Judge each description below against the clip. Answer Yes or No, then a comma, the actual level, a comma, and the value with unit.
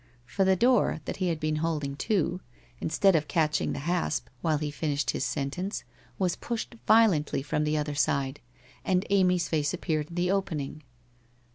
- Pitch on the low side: No, medium, 160 Hz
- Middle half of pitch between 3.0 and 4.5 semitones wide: Yes, average, 3.8 semitones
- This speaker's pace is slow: No, average, 175 wpm